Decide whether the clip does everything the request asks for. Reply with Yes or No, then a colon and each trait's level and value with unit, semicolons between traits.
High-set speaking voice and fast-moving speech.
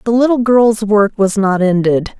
No: high, 210 Hz; average, 190 wpm